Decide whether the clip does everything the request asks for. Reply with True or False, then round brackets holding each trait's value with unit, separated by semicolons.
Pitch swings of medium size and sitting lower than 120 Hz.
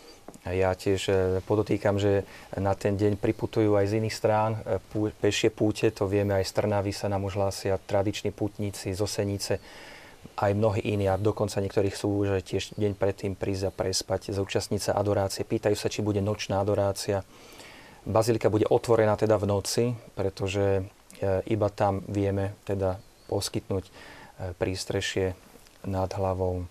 False (1.5 semitones; 100 Hz)